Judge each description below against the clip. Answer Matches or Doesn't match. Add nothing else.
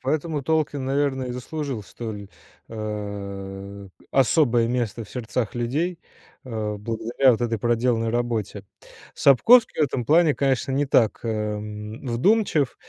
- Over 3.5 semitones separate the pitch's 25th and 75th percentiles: Matches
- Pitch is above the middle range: Doesn't match